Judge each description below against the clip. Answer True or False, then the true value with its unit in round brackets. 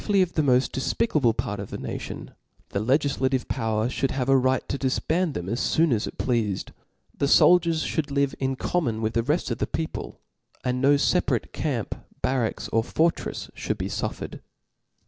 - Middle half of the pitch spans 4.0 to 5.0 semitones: True (4.3 semitones)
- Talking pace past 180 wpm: True (190 wpm)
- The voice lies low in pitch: True (130 Hz)